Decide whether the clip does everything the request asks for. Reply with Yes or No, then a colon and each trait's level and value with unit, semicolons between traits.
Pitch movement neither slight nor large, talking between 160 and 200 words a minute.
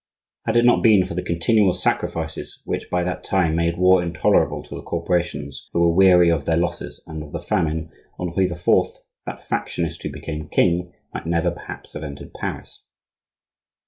No: narrow, 2.0 semitones; average, 175 wpm